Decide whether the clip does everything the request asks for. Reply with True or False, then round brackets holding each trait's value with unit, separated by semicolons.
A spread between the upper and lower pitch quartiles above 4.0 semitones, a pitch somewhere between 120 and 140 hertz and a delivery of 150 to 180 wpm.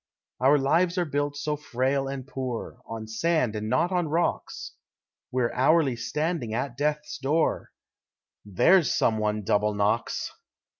False (4.9 semitones; 135 Hz; 140 wpm)